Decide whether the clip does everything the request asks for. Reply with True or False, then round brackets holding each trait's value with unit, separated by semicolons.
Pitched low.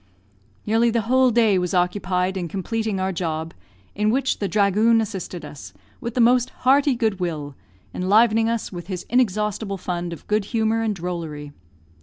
False (205 Hz)